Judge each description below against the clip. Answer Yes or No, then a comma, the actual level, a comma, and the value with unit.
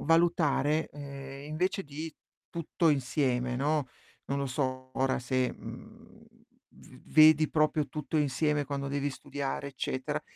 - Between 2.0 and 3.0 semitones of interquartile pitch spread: Yes, narrow, 2.4 semitones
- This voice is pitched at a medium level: Yes, medium, 145 Hz